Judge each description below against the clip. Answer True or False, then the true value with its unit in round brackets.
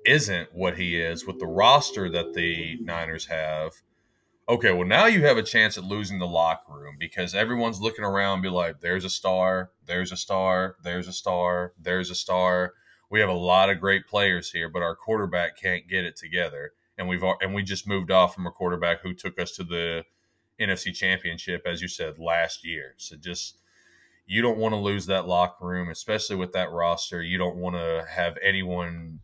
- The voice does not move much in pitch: True (1.8 semitones)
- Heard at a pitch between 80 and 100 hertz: True (90 Hz)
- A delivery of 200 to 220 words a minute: True (205 wpm)